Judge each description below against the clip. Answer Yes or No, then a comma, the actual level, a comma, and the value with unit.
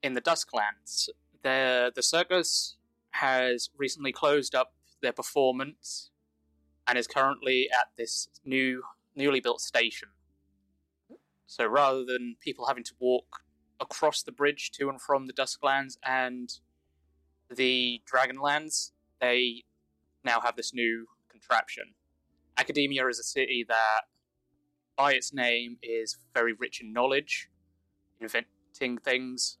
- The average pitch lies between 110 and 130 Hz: Yes, low, 120 Hz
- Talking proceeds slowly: Yes, slow, 120 wpm